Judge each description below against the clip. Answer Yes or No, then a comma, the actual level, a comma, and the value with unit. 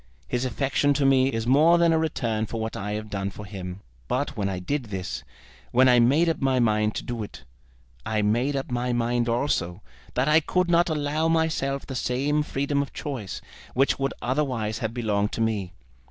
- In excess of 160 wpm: Yes, average, 200 wpm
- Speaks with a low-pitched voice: Yes, low, 125 Hz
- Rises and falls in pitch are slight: No, average, 4.9 semitones